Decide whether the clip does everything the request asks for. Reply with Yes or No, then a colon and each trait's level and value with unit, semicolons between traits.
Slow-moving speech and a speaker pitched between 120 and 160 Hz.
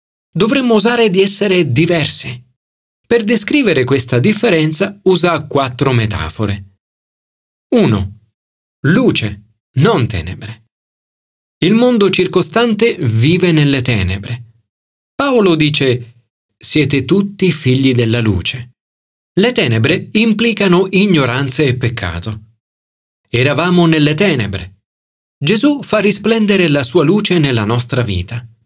Yes: slow, 100 wpm; low, 135 Hz